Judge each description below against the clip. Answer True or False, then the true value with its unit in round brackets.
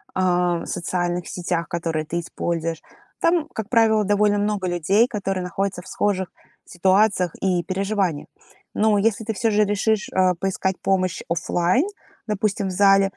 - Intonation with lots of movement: False (2.7 semitones)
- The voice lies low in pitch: False (190 Hz)